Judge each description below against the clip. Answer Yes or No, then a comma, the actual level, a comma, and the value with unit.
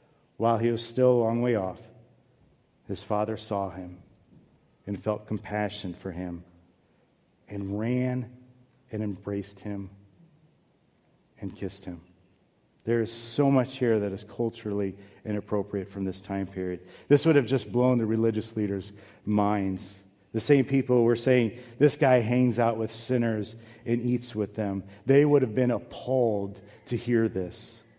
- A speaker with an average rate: Yes, average, 150 wpm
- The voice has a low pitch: Yes, low, 110 Hz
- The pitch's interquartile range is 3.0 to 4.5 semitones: Yes, average, 3.8 semitones